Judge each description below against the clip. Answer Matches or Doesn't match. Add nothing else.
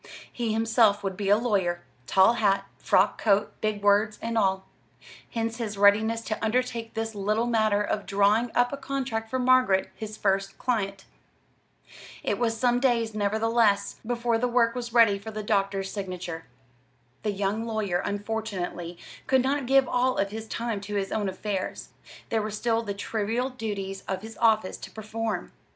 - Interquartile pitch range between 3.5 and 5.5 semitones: Doesn't match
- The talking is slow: Doesn't match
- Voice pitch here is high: Matches